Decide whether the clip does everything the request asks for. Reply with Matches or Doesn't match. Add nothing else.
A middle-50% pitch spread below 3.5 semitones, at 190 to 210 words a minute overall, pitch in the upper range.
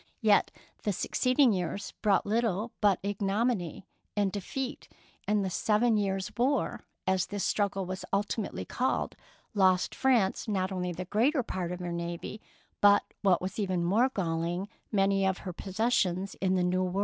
Doesn't match